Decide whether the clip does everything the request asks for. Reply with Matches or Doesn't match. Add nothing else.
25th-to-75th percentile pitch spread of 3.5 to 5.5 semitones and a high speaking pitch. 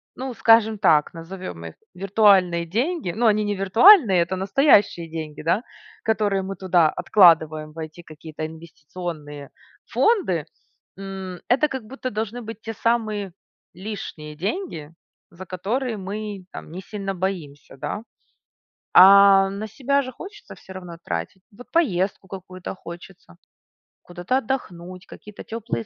Matches